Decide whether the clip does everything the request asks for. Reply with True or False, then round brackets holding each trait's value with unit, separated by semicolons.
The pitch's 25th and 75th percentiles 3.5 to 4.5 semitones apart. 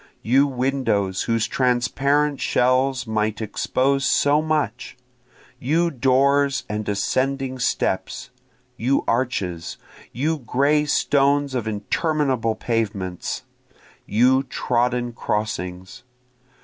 True (4.0 semitones)